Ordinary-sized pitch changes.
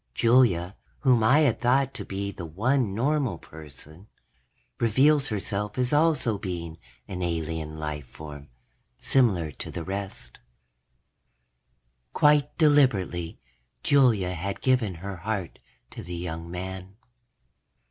No: wide, 7.0 semitones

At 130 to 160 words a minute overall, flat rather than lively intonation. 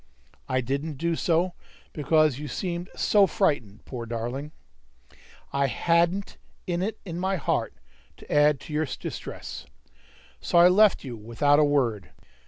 No: average, 140 wpm; average, 4.9 semitones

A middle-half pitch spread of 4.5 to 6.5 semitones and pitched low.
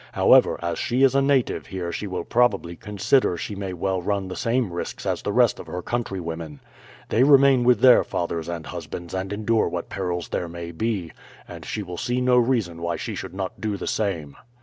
Yes: wide, 5.6 semitones; very low, 95 Hz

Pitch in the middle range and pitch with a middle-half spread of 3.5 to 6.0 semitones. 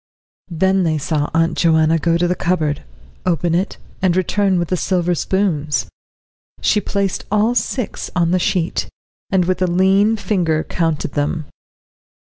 No: medium, 175 Hz; average, 2.8 semitones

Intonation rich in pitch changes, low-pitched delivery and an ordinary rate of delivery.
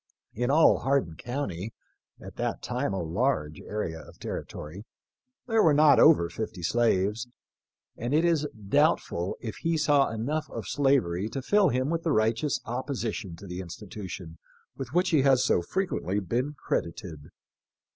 Yes: wide, 7.6 semitones; low, 120 Hz; average, 160 wpm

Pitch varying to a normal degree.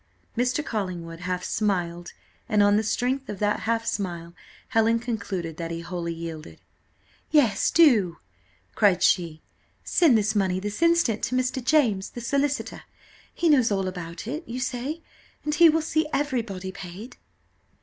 No: wide, 6.0 semitones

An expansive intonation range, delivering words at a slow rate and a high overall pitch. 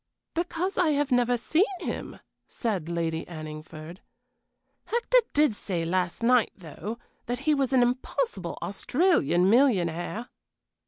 Yes: wide, 8.9 semitones; slow, 120 wpm; high, 235 Hz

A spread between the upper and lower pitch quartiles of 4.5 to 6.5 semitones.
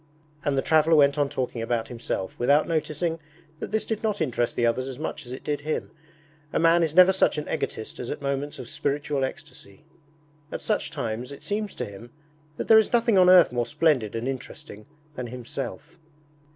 Yes: average, 5.1 semitones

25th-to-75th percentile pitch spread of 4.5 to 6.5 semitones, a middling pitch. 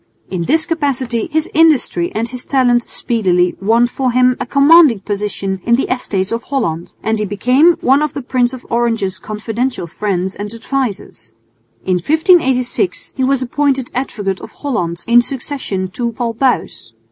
No: average, 4.8 semitones; high, 240 Hz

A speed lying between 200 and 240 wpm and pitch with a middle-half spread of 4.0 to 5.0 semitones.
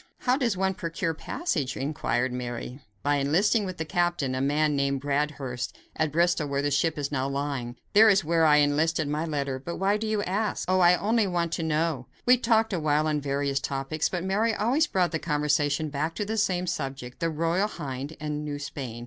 Yes: fast, 205 wpm; average, 4.5 semitones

